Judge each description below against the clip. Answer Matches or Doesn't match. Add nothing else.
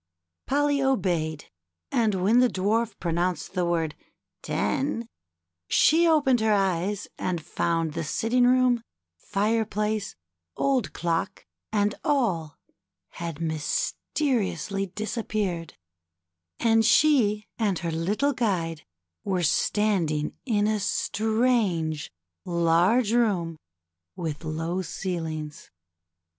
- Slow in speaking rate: Matches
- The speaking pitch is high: Matches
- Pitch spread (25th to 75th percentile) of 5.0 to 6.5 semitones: Matches